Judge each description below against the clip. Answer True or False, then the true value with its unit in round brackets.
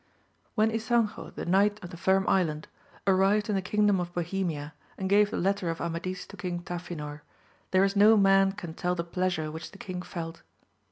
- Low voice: False (185 Hz)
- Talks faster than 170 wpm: True (190 wpm)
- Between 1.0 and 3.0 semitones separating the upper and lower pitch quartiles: True (2.7 semitones)